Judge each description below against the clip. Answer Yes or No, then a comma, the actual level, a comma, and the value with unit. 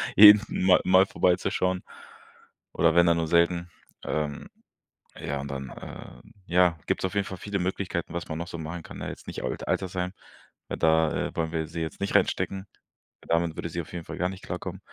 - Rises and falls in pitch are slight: Yes, narrow, 2.3 semitones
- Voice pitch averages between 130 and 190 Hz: No, very low, 85 Hz